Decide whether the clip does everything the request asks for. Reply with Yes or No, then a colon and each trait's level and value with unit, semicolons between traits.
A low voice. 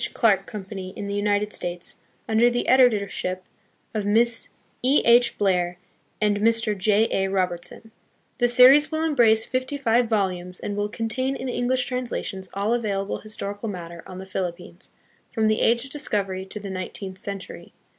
No: high, 210 Hz